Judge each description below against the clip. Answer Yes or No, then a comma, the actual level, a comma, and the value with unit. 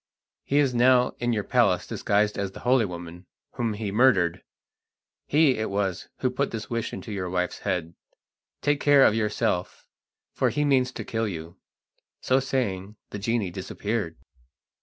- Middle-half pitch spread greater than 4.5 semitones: Yes, average, 5.2 semitones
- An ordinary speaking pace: Yes, average, 160 wpm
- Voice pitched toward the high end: No, low, 110 Hz